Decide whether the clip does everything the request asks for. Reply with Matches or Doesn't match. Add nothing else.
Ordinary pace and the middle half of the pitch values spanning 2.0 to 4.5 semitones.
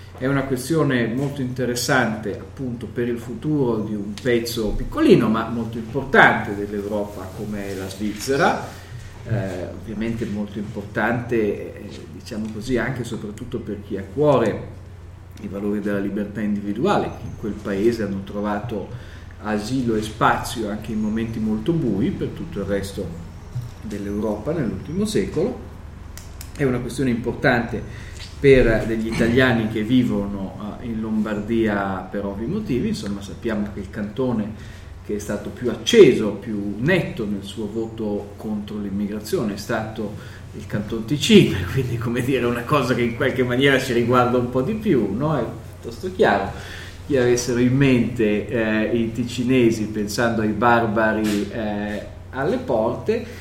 Matches